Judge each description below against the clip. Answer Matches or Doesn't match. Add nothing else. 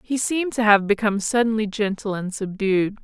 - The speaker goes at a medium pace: Matches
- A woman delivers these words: Matches